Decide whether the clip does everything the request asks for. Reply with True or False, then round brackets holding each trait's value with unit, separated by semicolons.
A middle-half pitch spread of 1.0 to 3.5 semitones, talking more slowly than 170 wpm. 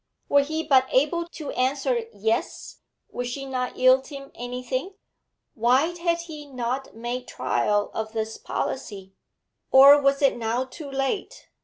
True (2.8 semitones; 145 wpm)